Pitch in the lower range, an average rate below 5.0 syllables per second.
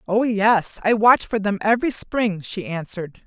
No: high, 205 Hz; 4.6 syllables/s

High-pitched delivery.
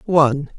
No: medium, 155 Hz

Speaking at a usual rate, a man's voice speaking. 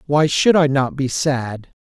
Yes: average, 190 wpm; male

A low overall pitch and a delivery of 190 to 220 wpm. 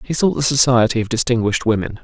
Yes: low, 120 Hz; fast, 205 wpm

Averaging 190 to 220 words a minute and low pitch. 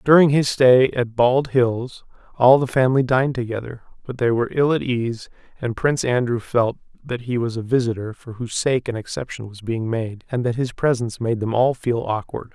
Yes: fast, 205 wpm; low, 120 Hz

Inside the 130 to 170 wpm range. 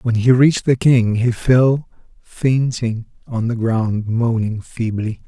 Yes: average, 150 wpm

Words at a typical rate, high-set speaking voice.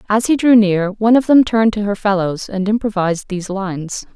No: fast, 215 wpm; high, 205 Hz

